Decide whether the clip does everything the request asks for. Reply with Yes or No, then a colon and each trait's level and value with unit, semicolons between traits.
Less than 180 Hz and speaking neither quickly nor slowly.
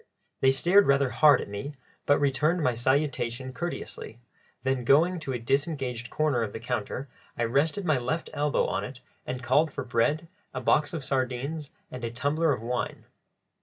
Yes: low, 135 Hz; average, 175 wpm